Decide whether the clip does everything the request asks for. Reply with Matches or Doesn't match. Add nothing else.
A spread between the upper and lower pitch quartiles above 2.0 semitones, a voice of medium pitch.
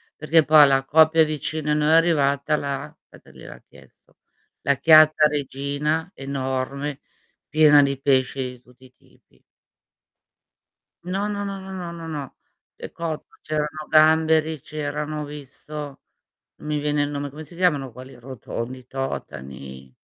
Matches